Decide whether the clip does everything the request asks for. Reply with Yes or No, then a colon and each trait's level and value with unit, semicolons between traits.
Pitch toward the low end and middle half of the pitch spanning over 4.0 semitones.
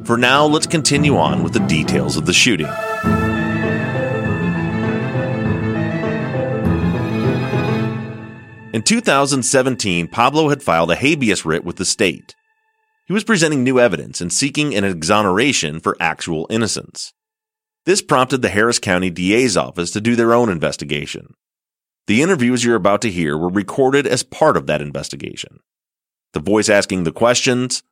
Yes: low, 115 Hz; average, 4.7 semitones